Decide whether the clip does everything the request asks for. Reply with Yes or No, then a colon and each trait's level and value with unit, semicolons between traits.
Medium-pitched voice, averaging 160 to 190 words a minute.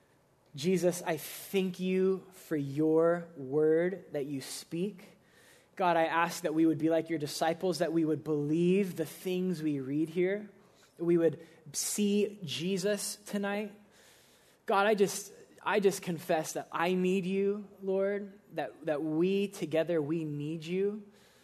No: medium, 175 Hz; average, 150 wpm